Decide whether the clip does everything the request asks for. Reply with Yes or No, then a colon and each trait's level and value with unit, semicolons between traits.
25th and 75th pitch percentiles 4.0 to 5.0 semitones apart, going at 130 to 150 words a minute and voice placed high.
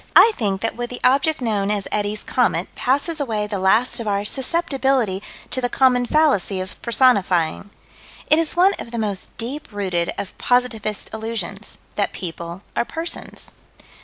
No: average, 4.6 semitones; average, 160 wpm; high, 225 Hz